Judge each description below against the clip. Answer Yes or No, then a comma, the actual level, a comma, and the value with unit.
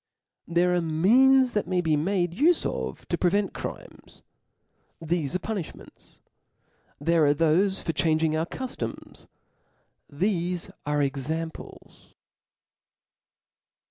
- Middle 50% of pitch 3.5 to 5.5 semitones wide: Yes, average, 3.8 semitones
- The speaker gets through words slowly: Yes, slow, 105 wpm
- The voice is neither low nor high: Yes, medium, 170 Hz